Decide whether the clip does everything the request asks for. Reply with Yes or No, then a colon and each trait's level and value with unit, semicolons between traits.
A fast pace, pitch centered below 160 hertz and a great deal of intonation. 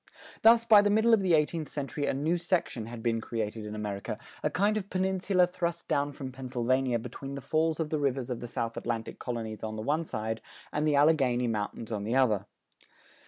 Yes: fast, 210 wpm; low, 135 Hz; wide, 6.4 semitones